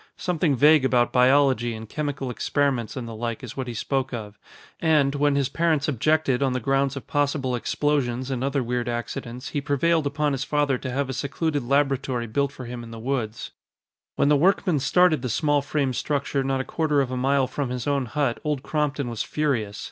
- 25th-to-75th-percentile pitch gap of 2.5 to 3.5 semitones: Yes, average, 2.8 semitones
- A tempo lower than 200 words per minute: No, fast, 205 wpm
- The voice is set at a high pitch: No, low, 135 Hz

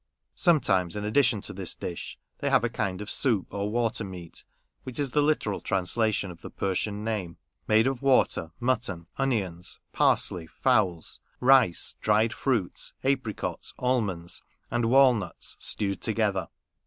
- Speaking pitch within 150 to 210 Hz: No, low, 110 Hz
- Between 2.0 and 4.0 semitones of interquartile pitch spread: No, average, 4.9 semitones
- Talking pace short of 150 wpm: Yes, average, 140 wpm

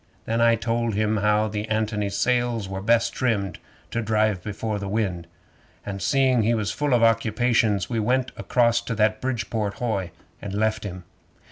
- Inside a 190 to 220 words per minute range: No, average, 170 wpm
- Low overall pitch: Yes, low, 110 Hz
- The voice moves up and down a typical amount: No, narrow, 2.3 semitones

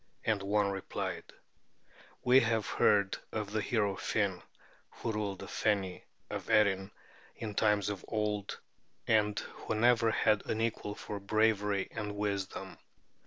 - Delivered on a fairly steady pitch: Yes, narrow, 1.6 semitones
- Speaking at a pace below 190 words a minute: Yes, slow, 135 wpm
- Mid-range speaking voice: No, low, 105 Hz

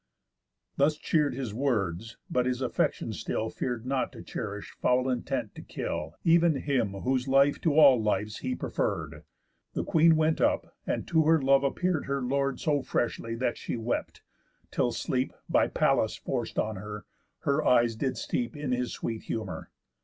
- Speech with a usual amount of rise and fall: Yes, average, 3.8 semitones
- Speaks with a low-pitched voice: Yes, low, 130 Hz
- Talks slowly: No, average, 170 wpm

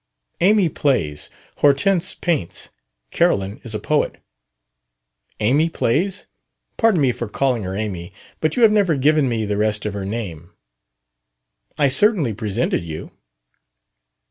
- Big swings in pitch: Yes, wide, 7.7 semitones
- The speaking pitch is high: No, low, 125 Hz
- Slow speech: Yes, slow, 130 wpm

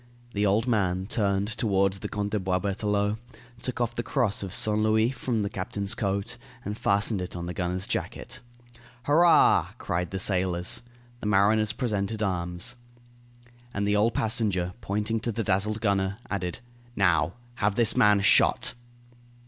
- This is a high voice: No, low, 100 Hz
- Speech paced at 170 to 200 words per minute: No, average, 155 wpm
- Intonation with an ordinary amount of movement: No, narrow, 2.3 semitones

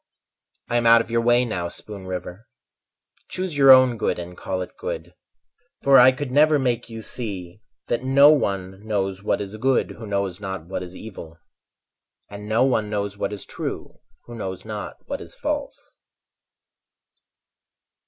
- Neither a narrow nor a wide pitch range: Yes, average, 4.4 semitones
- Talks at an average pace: Yes, average, 165 wpm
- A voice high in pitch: No, low, 110 Hz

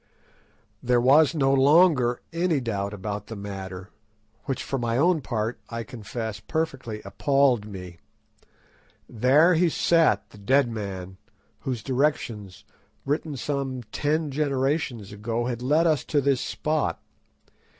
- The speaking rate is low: Yes, slow, 130 wpm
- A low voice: Yes, low, 125 Hz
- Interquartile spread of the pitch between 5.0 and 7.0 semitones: Yes, wide, 5.4 semitones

